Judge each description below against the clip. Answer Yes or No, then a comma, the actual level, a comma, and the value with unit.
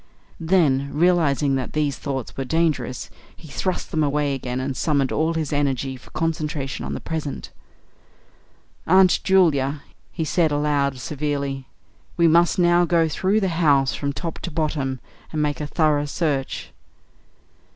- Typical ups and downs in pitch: Yes, average, 3.1 semitones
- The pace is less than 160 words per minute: Yes, average, 150 wpm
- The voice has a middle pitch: Yes, medium, 150 Hz